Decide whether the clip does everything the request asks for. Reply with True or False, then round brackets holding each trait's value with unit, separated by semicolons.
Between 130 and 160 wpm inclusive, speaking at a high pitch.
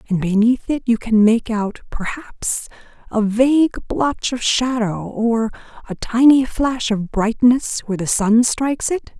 True (155 wpm; 235 Hz)